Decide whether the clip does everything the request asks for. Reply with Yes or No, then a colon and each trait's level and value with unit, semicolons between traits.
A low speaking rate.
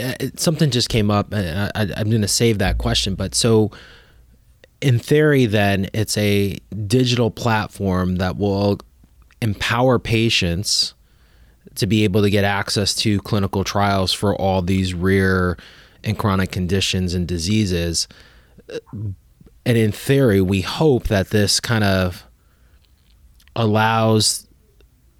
Yes: slow, 125 wpm